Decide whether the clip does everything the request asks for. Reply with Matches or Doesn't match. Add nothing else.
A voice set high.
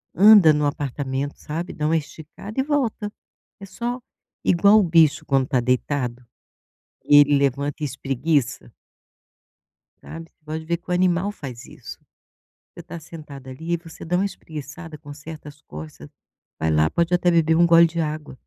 Doesn't match